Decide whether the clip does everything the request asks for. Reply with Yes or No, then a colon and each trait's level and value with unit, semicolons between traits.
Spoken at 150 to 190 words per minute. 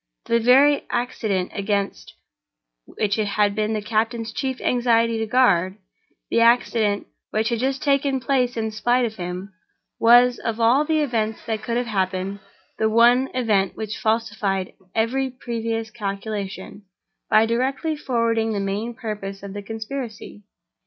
No: average, 140 wpm